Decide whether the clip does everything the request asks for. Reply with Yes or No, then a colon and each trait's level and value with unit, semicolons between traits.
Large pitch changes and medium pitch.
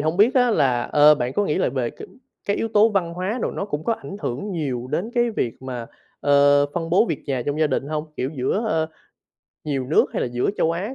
Yes: wide, 7.1 semitones; medium, 155 Hz